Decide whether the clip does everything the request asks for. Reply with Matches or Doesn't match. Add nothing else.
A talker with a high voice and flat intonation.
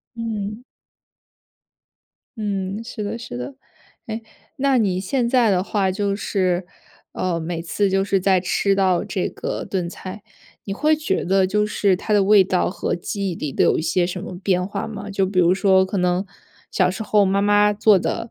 Matches